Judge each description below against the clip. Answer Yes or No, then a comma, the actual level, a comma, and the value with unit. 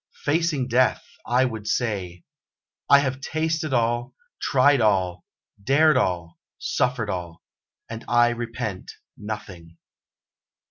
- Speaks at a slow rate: Yes, slow, 105 wpm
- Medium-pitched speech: No, low, 120 Hz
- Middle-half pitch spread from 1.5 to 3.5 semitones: No, average, 5.2 semitones